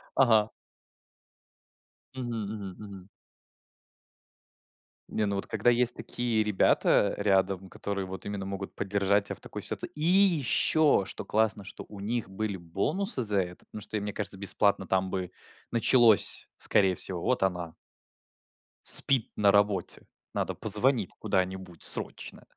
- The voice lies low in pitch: Yes, low, 100 Hz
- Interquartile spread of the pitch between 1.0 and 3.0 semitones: Yes, average, 2.7 semitones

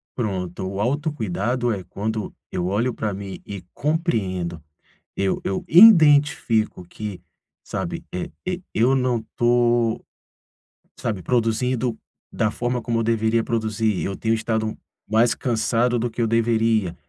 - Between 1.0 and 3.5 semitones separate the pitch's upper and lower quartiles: Yes, average, 2.8 semitones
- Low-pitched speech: Yes, low, 115 Hz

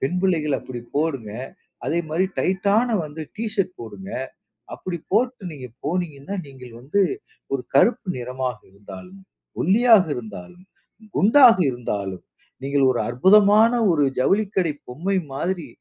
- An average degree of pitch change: No, wide, 7.6 semitones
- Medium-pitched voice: Yes, medium, 155 Hz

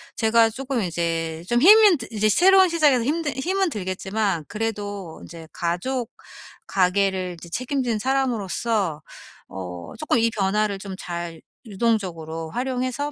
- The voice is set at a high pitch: Yes, high, 215 Hz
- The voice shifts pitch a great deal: Yes, wide, 6.5 semitones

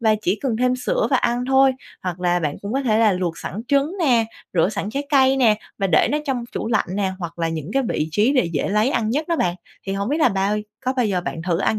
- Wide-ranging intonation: Yes, wide, 6.1 semitones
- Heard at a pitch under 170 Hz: No, high, 215 Hz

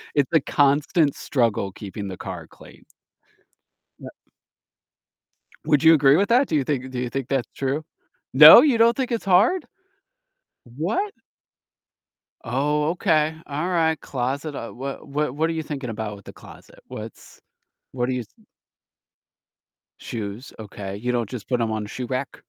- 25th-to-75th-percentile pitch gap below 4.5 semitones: No, average, 5.0 semitones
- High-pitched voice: No, low, 135 Hz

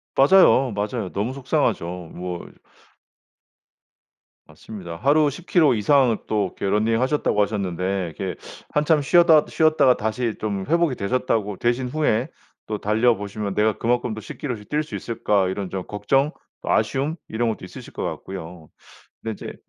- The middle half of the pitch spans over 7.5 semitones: No, average, 5.3 semitones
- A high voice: No, low, 110 Hz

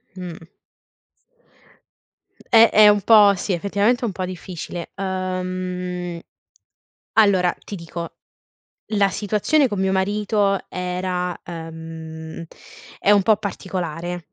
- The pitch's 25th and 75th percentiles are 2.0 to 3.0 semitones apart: Yes, narrow, 2.5 semitones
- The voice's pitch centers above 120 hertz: Yes, medium, 185 Hz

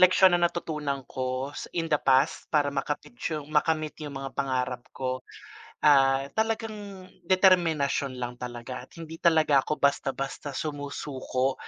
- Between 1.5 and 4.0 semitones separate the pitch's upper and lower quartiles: Yes, average, 3.4 semitones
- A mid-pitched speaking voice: Yes, medium, 145 Hz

